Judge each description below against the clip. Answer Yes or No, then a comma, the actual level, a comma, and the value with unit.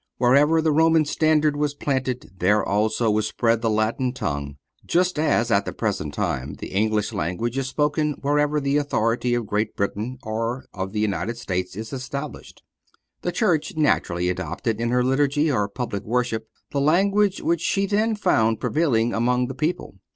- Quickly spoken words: No, average, 170 wpm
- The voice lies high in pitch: No, low, 125 Hz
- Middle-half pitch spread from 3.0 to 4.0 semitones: No, wide, 5.5 semitones